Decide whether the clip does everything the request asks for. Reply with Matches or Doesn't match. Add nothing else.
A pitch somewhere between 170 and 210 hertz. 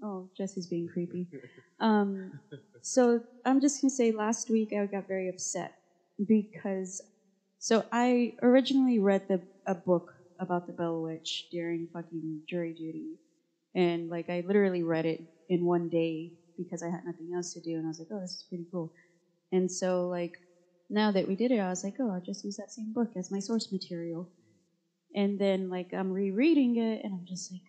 Matches